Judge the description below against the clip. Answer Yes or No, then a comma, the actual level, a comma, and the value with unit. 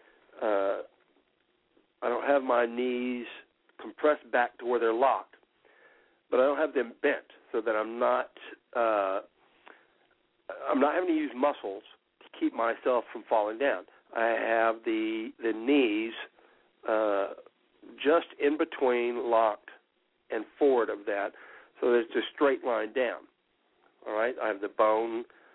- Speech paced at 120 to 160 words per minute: Yes, average, 145 wpm